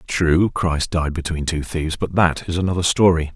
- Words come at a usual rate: Yes, average, 195 wpm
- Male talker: Yes, male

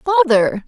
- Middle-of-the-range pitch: No, very high, 280 Hz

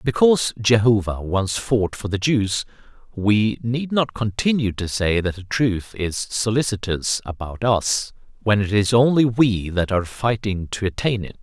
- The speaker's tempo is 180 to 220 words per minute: No, average, 165 wpm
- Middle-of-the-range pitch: No, low, 110 Hz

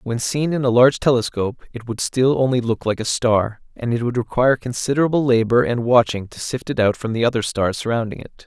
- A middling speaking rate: No, fast, 225 wpm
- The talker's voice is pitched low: Yes, low, 120 Hz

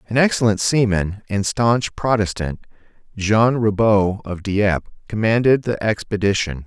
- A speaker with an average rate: No, slow, 115 wpm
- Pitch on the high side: No, low, 105 Hz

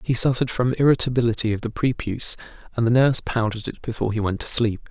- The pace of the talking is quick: Yes, fast, 210 wpm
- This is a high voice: No, low, 115 Hz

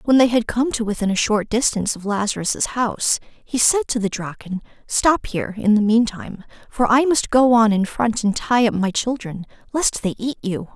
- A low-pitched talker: No, high, 225 Hz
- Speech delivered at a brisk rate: Yes, fast, 210 wpm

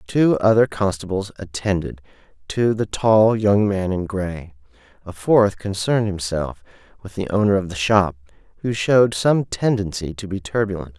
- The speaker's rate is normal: Yes, average, 155 wpm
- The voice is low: Yes, low, 100 Hz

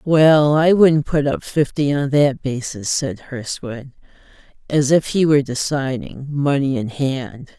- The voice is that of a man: No, female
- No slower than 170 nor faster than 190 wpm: No, average, 150 wpm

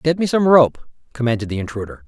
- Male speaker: Yes, male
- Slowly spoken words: No, average, 200 wpm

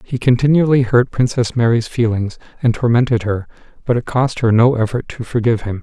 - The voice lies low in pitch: Yes, low, 120 Hz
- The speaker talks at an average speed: Yes, average, 185 wpm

